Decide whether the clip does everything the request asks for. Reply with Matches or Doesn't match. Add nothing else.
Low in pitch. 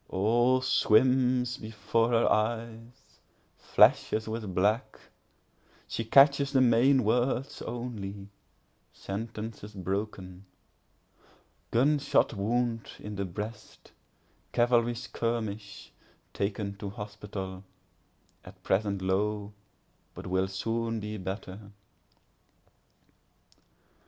Matches